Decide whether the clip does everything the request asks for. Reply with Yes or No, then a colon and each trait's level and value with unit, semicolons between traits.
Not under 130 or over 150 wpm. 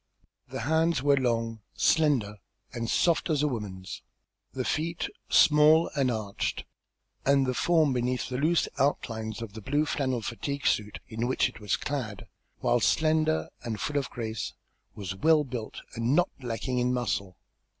No: average, 160 wpm